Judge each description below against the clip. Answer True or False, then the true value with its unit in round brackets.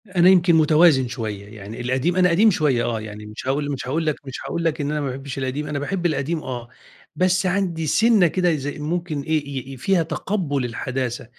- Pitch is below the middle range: False (150 Hz)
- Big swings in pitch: False (4.9 semitones)